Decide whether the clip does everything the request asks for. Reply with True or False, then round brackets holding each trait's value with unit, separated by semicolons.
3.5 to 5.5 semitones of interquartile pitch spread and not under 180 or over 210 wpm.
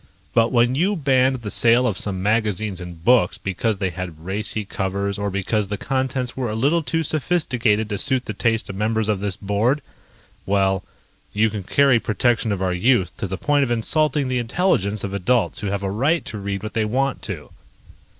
True (4.4 semitones; 200 wpm)